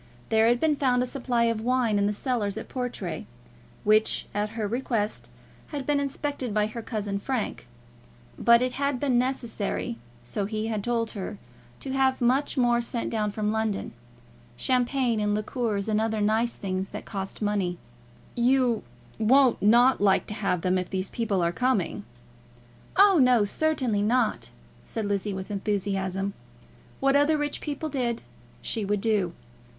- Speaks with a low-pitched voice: No, high, 225 Hz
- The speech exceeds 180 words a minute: No, average, 160 wpm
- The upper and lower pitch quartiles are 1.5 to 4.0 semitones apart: Yes, average, 3.7 semitones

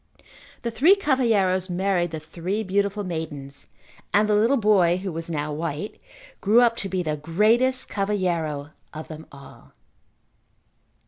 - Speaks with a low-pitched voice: No, medium, 185 Hz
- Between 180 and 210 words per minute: No, average, 140 wpm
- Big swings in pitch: No, average, 4.8 semitones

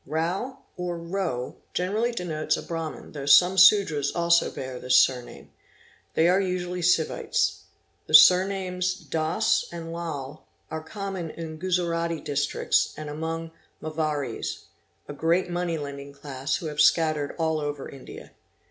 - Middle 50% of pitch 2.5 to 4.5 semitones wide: Yes, average, 3.2 semitones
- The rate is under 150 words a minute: Yes, slow, 135 wpm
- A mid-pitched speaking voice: Yes, medium, 165 Hz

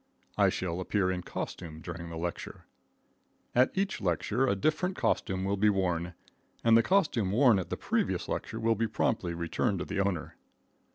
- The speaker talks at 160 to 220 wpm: Yes, average, 175 wpm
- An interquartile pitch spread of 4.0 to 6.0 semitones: Yes, average, 4.7 semitones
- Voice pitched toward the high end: No, very low, 95 Hz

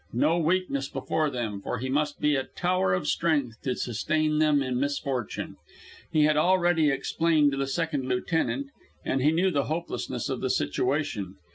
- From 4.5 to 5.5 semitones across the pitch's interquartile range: No, average, 3.7 semitones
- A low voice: No, medium, 145 Hz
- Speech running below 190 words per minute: Yes, average, 165 wpm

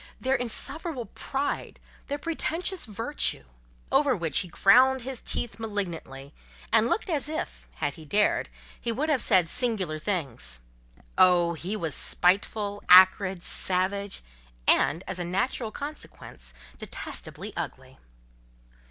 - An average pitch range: No, wide, 6.7 semitones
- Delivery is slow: Yes, slow, 125 wpm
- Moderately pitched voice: No, high, 205 Hz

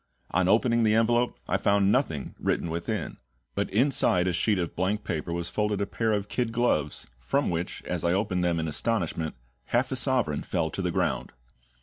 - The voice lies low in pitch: Yes, low, 100 Hz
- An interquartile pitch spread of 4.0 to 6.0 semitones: Yes, average, 5.2 semitones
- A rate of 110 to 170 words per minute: No, average, 195 wpm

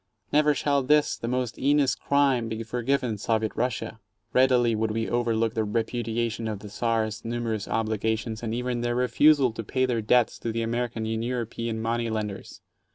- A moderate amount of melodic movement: No, narrow, 2.0 semitones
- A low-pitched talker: Yes, low, 115 Hz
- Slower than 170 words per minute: No, average, 175 wpm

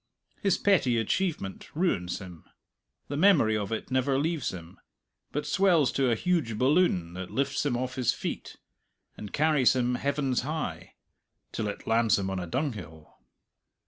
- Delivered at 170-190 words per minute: No, average, 155 wpm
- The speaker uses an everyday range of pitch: No, wide, 6.3 semitones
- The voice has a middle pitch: No, low, 130 Hz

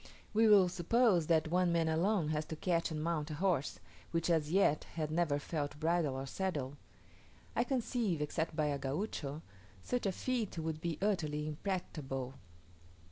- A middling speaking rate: Yes, average, 165 wpm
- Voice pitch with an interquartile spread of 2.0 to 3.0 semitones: No, average, 3.8 semitones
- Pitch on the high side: No, medium, 165 Hz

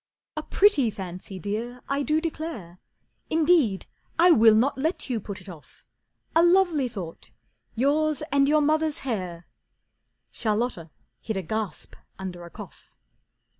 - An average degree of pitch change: No, wide, 8.1 semitones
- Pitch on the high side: Yes, high, 245 Hz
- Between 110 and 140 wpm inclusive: Yes, slow, 135 wpm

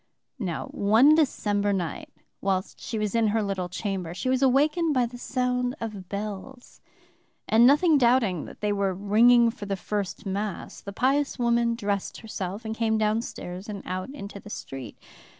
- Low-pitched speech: No, high, 215 Hz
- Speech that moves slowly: No, average, 170 wpm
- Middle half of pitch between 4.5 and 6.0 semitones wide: No, average, 3.8 semitones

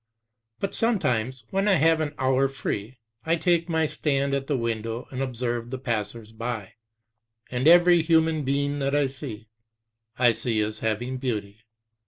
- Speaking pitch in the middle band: No, low, 130 Hz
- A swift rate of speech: No, average, 160 wpm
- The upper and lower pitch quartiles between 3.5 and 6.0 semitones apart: Yes, average, 5.1 semitones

